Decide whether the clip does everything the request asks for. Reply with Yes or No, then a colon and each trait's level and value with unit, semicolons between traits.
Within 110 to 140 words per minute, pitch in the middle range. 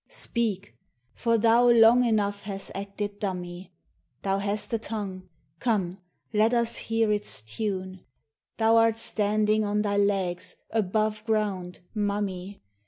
No: slow, 135 wpm; high, 205 Hz